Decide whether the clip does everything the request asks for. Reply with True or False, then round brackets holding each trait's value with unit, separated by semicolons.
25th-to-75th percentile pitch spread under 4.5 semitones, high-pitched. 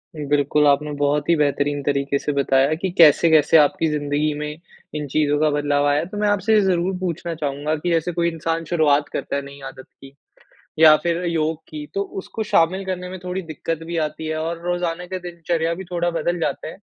False (2.9 semitones; 155 Hz)